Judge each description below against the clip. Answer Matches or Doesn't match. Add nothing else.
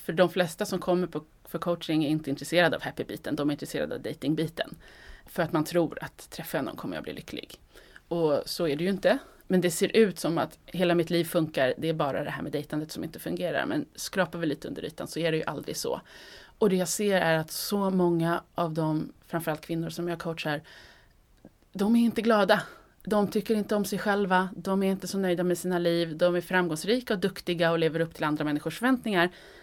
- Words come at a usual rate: Doesn't match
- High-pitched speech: Doesn't match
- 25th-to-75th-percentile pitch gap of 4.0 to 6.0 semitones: Doesn't match